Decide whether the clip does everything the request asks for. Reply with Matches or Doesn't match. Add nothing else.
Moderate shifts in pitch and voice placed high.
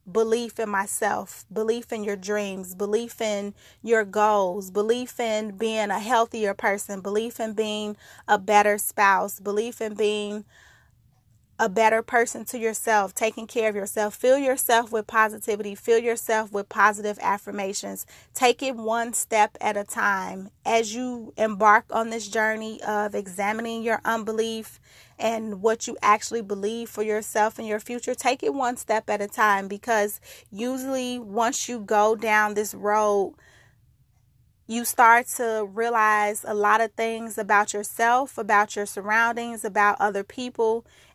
Doesn't match